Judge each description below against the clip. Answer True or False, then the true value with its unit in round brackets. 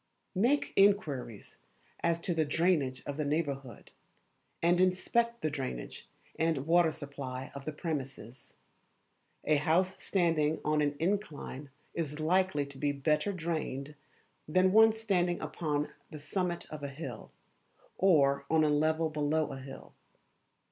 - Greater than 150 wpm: False (135 wpm)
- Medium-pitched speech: True (155 Hz)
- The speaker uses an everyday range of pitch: True (3.6 semitones)